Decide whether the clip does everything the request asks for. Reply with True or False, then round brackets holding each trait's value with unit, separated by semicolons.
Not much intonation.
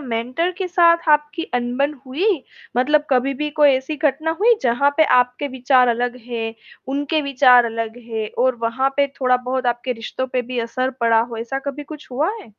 False (3.3 semitones)